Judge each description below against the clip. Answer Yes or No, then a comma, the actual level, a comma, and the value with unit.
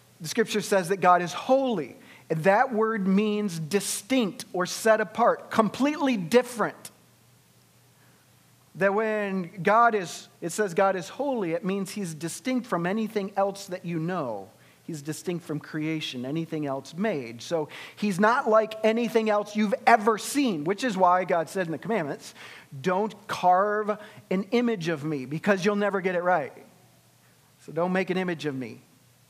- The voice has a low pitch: No, high, 190 Hz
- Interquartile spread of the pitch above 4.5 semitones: Yes, average, 5.0 semitones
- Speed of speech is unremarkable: Yes, average, 160 wpm